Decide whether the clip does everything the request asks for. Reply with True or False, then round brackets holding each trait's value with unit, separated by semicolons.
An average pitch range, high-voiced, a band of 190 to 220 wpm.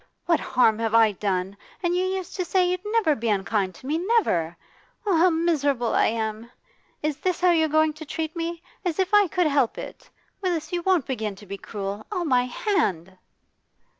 False (8.3 semitones; 310 Hz; 195 wpm)